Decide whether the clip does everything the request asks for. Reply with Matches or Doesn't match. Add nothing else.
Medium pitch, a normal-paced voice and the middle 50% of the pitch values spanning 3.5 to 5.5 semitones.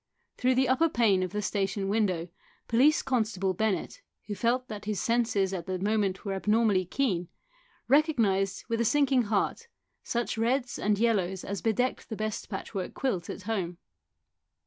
Doesn't match